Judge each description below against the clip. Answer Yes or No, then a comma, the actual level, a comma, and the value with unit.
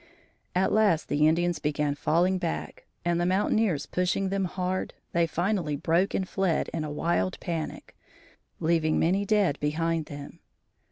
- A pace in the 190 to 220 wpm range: No, average, 150 wpm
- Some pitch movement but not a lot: Yes, average, 3.5 semitones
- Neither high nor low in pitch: Yes, medium, 170 Hz